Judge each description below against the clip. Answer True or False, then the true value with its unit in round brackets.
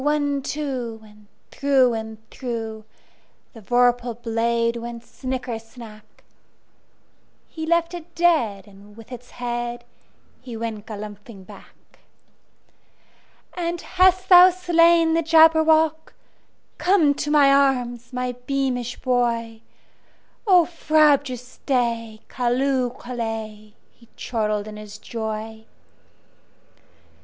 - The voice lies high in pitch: True (245 Hz)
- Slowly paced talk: True (90 wpm)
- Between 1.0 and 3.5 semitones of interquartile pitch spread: False (4.9 semitones)